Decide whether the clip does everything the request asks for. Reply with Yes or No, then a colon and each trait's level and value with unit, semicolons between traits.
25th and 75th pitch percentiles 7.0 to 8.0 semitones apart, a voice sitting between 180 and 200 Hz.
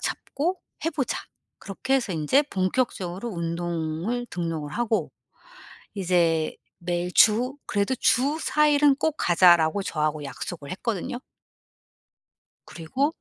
Yes: wide, 7.4 semitones; high, 190 Hz